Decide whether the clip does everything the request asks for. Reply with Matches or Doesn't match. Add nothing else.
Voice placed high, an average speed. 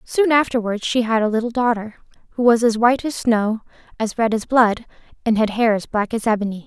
Doesn't match